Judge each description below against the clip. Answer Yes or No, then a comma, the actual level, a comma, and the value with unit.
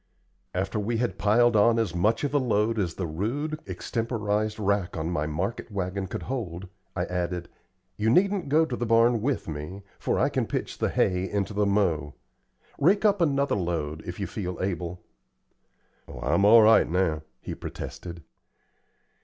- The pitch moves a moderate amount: Yes, average, 4.8 semitones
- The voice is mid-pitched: No, low, 100 Hz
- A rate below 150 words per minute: No, average, 170 wpm